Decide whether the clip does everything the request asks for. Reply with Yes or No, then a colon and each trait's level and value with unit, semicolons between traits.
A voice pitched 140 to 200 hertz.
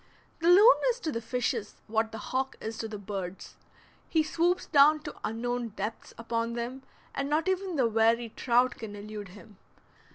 No: high, 235 Hz